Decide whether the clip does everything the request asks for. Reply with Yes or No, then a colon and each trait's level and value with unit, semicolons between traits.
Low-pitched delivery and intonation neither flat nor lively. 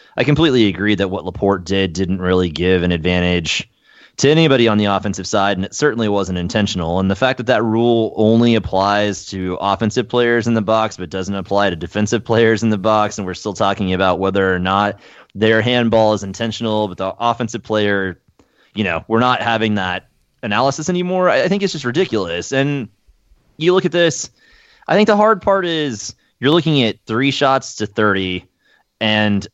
Yes: low, 105 Hz; average, 4.2 semitones